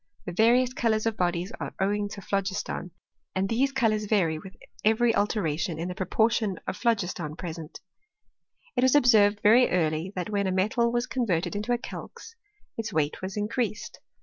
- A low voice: No, high, 205 Hz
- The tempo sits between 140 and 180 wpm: Yes, average, 175 wpm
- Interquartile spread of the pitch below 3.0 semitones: No, average, 4.0 semitones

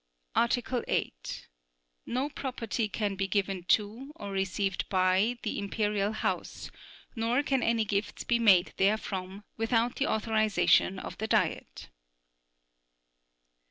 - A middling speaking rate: No, slow, 120 wpm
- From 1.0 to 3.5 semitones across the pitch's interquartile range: Yes, average, 3.1 semitones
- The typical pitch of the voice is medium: No, high, 215 Hz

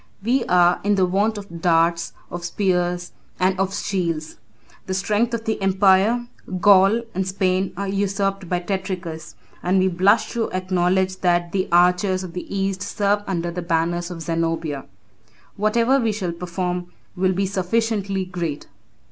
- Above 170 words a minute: No, average, 150 wpm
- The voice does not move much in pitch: Yes, narrow, 2.3 semitones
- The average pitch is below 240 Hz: Yes, medium, 185 Hz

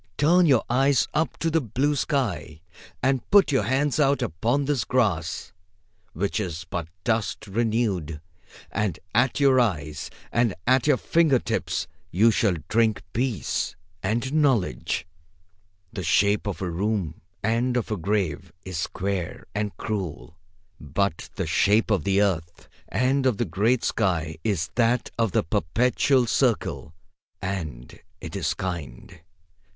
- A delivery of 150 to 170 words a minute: No, average, 140 wpm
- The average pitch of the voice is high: No, low, 110 Hz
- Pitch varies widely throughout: Yes, wide, 6.0 semitones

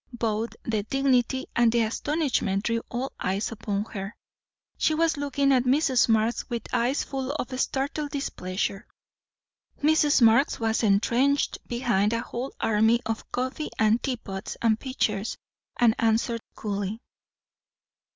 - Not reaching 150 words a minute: Yes, slow, 135 wpm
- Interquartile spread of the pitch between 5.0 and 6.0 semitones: No, average, 3.7 semitones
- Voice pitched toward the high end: Yes, high, 235 Hz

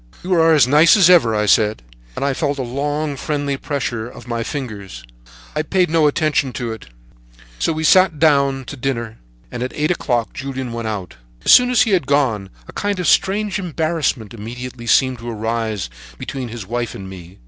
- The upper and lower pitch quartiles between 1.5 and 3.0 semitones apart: No, average, 5.1 semitones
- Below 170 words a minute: No, average, 200 wpm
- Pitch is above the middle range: No, low, 135 Hz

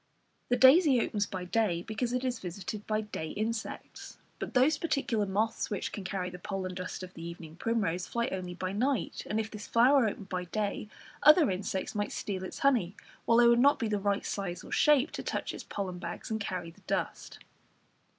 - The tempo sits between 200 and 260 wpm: Yes, fast, 205 wpm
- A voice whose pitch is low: No, high, 210 Hz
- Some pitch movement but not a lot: Yes, average, 4.3 semitones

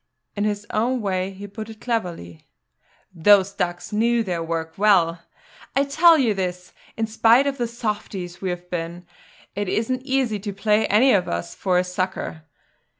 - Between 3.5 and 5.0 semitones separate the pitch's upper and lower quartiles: Yes, average, 4.1 semitones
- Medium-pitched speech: No, high, 205 Hz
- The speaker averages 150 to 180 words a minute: Yes, average, 170 wpm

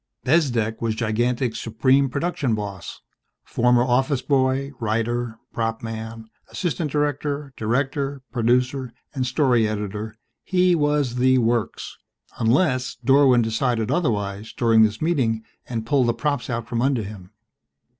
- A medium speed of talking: No, slow, 125 wpm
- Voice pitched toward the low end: Yes, low, 125 Hz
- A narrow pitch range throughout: No, average, 3.5 semitones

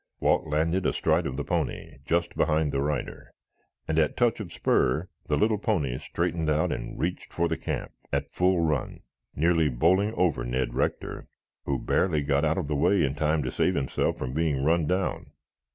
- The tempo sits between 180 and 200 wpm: Yes, average, 190 wpm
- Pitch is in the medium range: No, very low, 80 Hz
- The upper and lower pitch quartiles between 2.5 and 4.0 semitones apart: Yes, average, 3.6 semitones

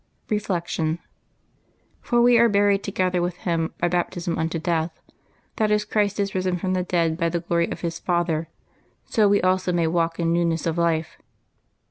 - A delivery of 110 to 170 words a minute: No, average, 185 wpm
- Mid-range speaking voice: Yes, medium, 175 Hz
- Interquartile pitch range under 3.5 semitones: Yes, average, 2.8 semitones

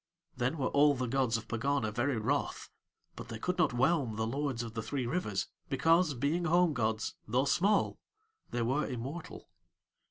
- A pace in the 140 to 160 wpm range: No, average, 170 wpm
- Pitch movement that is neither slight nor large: Yes, average, 4.5 semitones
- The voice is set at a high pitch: No, low, 135 Hz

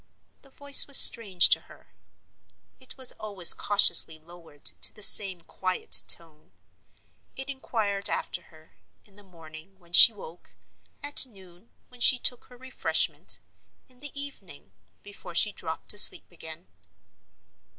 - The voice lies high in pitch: Yes, high, 200 Hz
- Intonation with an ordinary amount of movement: No, wide, 6.4 semitones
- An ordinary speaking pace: No, slow, 130 wpm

